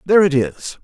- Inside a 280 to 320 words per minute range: No, fast, 215 wpm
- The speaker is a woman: No, male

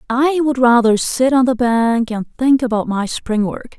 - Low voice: No, high, 240 Hz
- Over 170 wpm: Yes, fast, 205 wpm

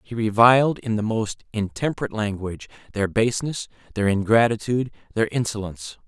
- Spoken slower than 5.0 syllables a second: No, 5.9 syllables/s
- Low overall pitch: Yes, low, 110 Hz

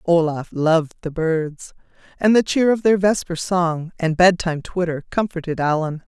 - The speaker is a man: No, female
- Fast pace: No, average, 155 wpm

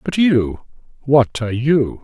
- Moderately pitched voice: No, low, 130 Hz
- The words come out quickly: No, slow, 120 wpm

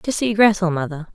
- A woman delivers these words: Yes, female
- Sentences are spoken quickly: Yes, fast, 210 wpm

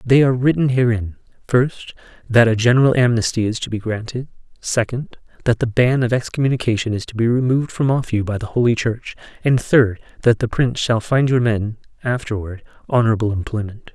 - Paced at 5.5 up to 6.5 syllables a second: Yes, 5.8 syllables/s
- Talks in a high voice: No, low, 120 Hz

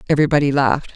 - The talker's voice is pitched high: No, medium, 140 Hz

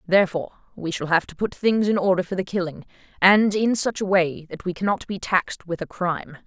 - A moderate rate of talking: No, fast, 230 wpm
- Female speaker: Yes, female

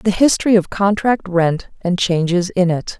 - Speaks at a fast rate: No, average, 180 wpm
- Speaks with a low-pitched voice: No, high, 190 Hz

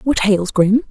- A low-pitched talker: No, high, 210 Hz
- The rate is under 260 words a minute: Yes, average, 200 wpm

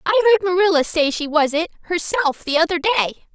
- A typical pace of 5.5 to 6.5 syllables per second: Yes, 5.9 syllables/s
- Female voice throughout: Yes, female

